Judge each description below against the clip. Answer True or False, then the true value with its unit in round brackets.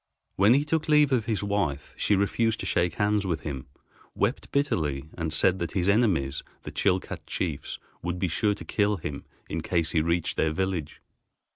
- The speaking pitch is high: False (95 Hz)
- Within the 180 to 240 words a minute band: True (185 wpm)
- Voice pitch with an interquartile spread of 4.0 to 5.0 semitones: True (4.6 semitones)